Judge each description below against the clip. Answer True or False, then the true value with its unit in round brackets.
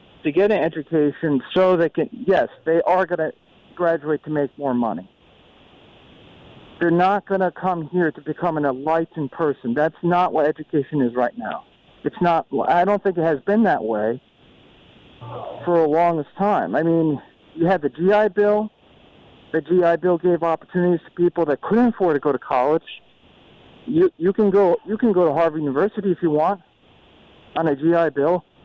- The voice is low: False (170 Hz)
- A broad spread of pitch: False (3.4 semitones)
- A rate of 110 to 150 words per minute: False (180 wpm)